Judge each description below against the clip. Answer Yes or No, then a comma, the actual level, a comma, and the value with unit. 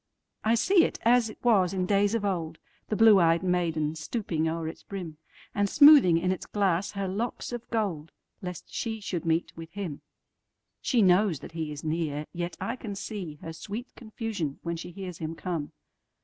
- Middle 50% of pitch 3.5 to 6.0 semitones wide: Yes, average, 4.6 semitones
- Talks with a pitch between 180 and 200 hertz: Yes, medium, 185 Hz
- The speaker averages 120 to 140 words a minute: No, average, 170 wpm